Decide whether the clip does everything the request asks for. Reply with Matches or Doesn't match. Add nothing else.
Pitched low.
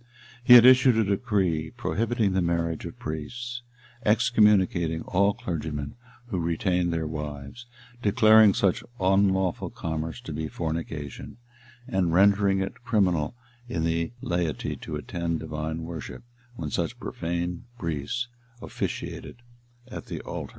Matches